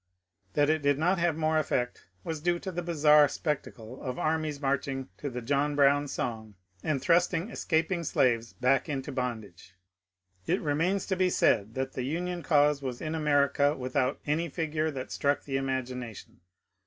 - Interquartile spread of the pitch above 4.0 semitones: No, average, 3.6 semitones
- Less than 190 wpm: Yes, average, 175 wpm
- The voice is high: No, medium, 145 Hz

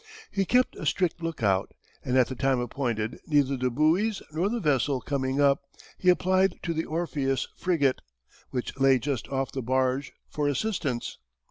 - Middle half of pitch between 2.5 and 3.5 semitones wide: No, average, 4.4 semitones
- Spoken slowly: No, average, 165 wpm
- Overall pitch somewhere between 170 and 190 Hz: No, medium, 140 Hz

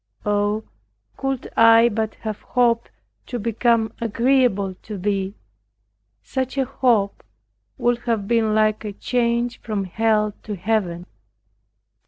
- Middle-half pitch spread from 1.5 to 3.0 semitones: Yes, narrow, 2.4 semitones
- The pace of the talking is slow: Yes, slow, 120 wpm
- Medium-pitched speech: No, high, 220 Hz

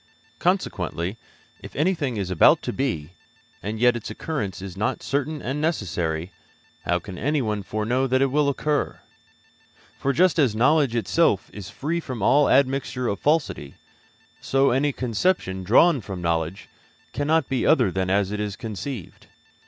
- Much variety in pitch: Yes, wide, 6.7 semitones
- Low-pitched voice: Yes, low, 120 Hz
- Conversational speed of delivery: Yes, average, 155 wpm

